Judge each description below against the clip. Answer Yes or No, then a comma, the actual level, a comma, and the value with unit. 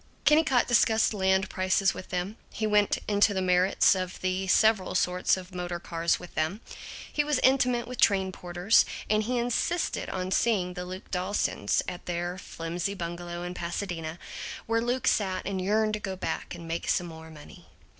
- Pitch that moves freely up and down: No, average, 3.3 semitones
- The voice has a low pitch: No, medium, 185 Hz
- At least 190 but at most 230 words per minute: No, average, 175 wpm